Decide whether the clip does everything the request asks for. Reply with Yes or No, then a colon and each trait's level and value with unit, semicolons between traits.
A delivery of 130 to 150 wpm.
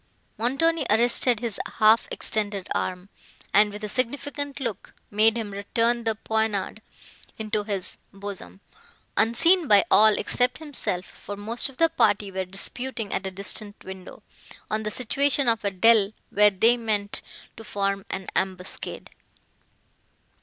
Yes: average, 140 wpm